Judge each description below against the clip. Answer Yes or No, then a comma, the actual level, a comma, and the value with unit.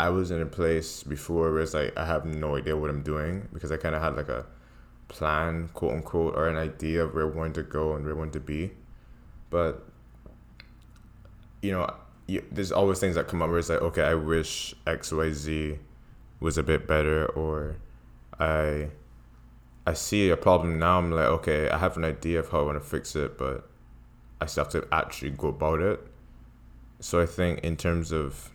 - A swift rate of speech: Yes, fast, 210 wpm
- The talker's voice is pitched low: Yes, very low, 80 Hz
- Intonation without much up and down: Yes, narrow, 1.9 semitones